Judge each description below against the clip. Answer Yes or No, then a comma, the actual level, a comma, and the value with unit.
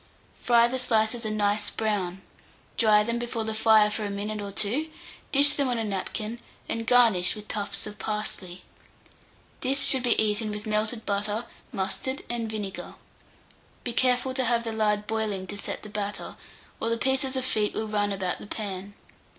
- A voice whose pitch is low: No, high, 215 Hz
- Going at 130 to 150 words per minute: No, average, 180 wpm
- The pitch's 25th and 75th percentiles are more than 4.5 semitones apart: No, narrow, 2.4 semitones